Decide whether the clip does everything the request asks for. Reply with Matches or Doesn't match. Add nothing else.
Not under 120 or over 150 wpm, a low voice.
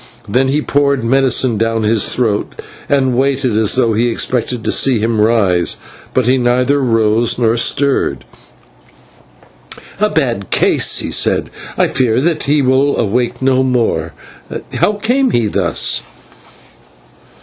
Matches